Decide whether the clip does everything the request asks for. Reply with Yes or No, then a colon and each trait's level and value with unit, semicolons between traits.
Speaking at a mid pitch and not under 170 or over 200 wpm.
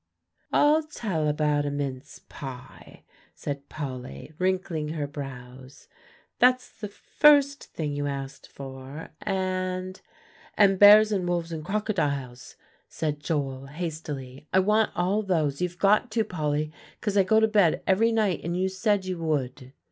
No: medium, 165 Hz; average, 145 wpm